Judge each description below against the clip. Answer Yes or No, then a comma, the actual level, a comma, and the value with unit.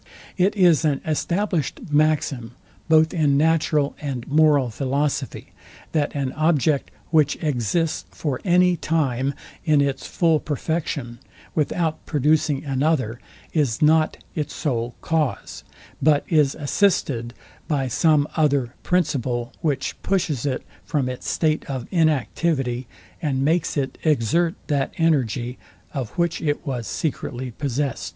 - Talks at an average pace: No, slow, 125 wpm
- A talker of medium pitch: Yes, medium, 145 Hz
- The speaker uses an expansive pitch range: No, average, 3.3 semitones